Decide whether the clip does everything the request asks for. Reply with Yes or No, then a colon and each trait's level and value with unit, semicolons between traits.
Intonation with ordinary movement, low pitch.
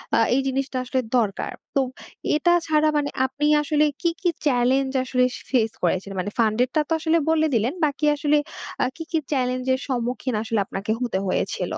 No: average, 3.8 semitones; very high, 260 Hz